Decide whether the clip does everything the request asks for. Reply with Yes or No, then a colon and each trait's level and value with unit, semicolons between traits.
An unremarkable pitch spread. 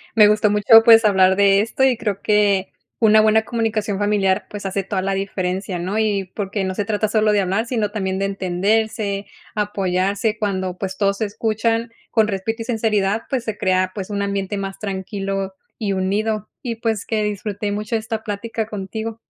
No: narrow, 2.1 semitones